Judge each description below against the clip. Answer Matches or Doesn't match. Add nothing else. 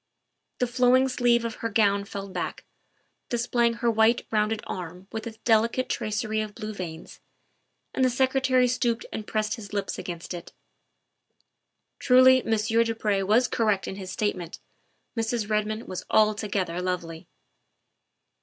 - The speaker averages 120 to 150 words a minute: Matches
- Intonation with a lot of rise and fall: Doesn't match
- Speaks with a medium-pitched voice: Doesn't match